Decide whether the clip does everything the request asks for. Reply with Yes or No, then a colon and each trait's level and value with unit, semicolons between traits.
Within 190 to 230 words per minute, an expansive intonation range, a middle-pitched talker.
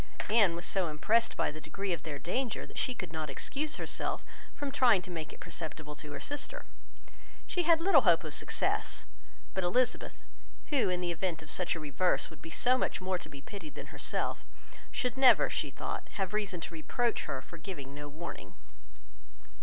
Yes: average, 195 wpm; wide, 7.0 semitones; medium, 180 Hz